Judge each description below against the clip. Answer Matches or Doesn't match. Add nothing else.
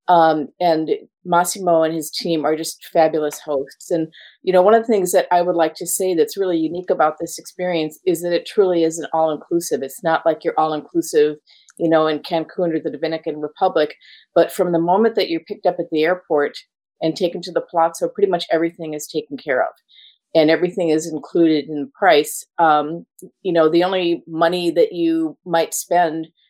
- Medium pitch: Matches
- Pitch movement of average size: Doesn't match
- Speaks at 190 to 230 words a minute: Matches